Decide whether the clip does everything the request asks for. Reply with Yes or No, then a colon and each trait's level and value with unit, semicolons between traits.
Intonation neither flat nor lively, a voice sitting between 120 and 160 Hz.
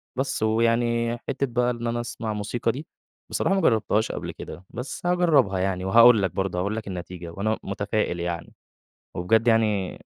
No: average, 3.6 semitones; low, 110 Hz